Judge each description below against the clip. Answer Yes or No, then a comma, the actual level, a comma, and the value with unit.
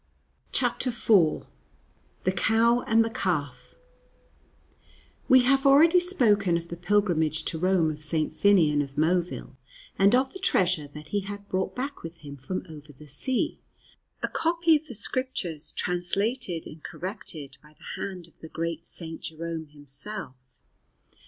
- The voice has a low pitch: No, medium, 180 Hz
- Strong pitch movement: Yes, wide, 6.3 semitones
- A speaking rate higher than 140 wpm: Yes, average, 150 wpm